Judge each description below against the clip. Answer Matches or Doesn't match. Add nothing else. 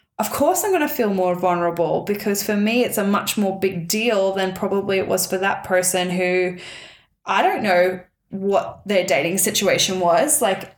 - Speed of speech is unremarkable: Matches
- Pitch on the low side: Doesn't match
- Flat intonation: Matches